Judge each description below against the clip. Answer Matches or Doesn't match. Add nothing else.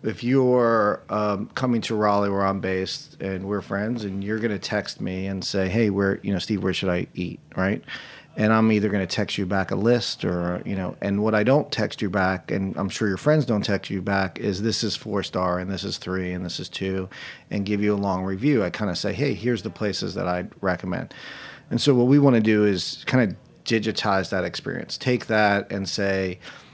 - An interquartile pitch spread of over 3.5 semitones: Doesn't match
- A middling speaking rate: Doesn't match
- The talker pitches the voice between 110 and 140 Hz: Doesn't match